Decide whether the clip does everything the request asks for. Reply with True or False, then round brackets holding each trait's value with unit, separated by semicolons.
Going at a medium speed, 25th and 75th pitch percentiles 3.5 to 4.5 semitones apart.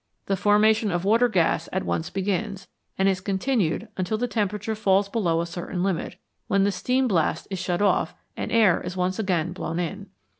False (195 wpm; 2.9 semitones)